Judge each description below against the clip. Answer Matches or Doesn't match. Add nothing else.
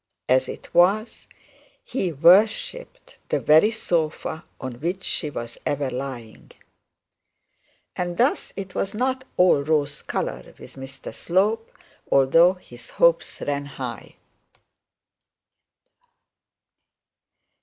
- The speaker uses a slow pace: Matches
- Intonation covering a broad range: Matches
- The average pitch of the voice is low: Doesn't match